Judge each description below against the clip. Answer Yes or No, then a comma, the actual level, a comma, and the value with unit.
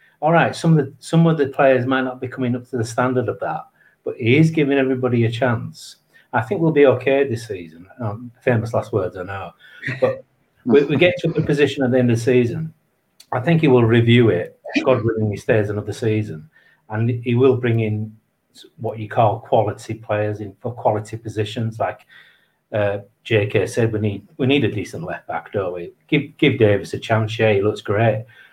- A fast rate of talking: Yes, fast, 210 wpm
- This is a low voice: Yes, low, 120 Hz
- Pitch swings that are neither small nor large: Yes, average, 3.8 semitones